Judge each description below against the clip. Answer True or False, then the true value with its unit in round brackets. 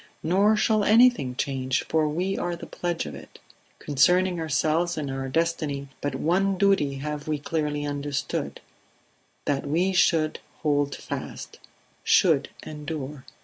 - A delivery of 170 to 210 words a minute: False (135 wpm)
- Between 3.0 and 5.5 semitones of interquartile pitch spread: True (3.7 semitones)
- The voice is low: False (155 Hz)